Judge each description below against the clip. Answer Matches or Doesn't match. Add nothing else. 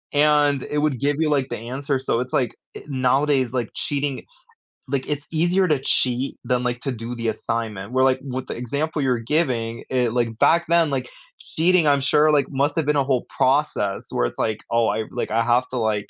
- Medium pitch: Doesn't match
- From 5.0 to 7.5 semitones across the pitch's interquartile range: Doesn't match